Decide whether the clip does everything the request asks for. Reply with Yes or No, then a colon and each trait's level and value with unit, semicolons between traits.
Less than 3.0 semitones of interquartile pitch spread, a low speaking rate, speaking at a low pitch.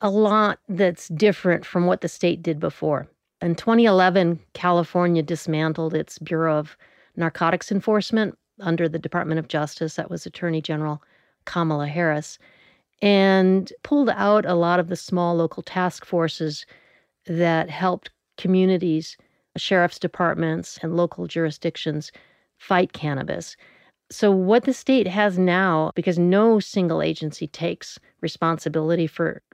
No: narrow, 2.6 semitones; slow, 130 wpm; medium, 175 Hz